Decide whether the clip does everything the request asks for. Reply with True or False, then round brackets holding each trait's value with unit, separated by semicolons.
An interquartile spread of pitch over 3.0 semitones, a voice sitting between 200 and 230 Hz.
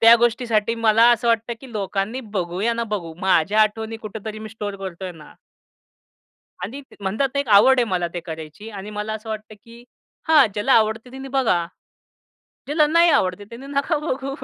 True (3.8 semitones; 220 Hz)